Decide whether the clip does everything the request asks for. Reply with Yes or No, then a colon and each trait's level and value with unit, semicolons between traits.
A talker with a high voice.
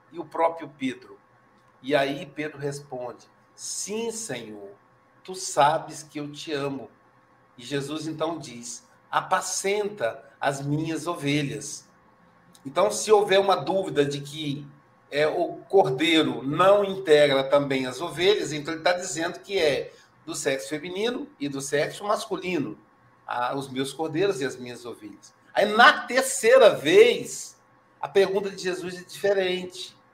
No: medium, 160 Hz